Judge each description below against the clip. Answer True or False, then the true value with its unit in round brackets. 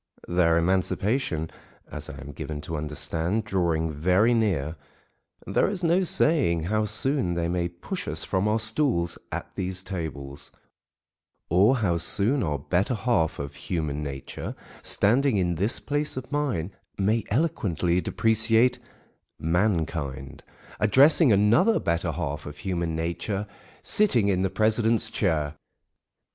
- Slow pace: True (130 wpm)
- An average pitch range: False (5.7 semitones)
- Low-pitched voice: True (95 Hz)